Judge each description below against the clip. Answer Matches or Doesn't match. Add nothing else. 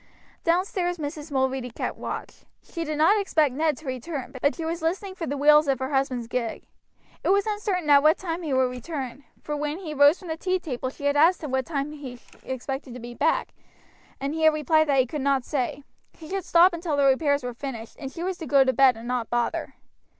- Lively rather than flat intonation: Doesn't match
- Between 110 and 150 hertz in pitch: Doesn't match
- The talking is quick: Matches